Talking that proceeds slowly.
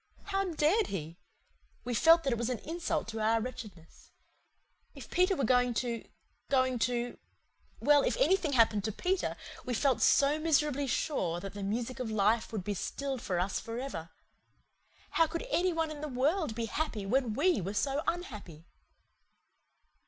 No: average, 170 wpm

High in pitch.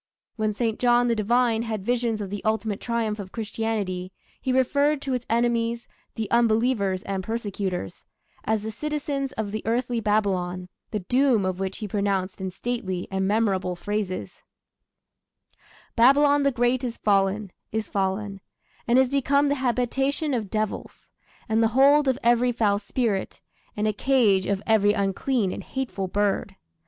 Yes: high, 220 Hz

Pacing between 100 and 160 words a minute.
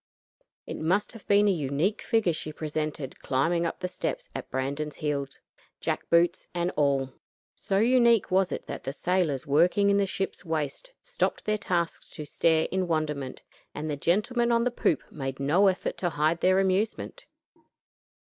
No: average, 170 wpm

